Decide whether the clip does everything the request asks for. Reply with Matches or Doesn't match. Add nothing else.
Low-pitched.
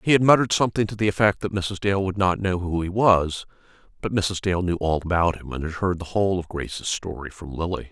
Matches